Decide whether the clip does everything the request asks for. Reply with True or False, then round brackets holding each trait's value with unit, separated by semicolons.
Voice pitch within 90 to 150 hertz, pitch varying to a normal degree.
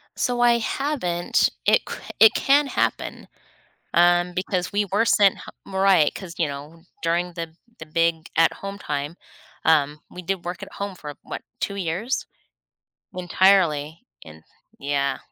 False (175 Hz; 3.6 semitones)